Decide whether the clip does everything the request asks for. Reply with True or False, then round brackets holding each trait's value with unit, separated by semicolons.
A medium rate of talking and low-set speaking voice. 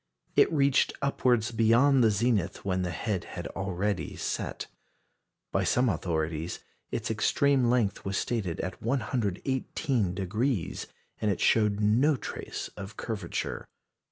False (125 wpm; 105 Hz)